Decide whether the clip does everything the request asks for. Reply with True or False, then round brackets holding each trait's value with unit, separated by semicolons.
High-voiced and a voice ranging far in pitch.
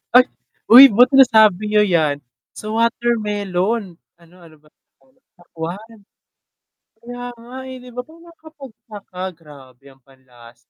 True (210 Hz; 7.1 semitones)